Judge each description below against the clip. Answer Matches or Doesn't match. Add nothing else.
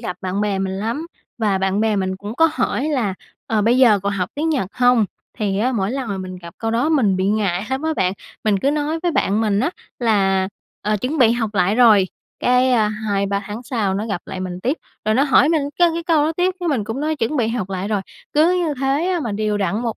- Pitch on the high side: Matches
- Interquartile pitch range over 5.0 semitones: Matches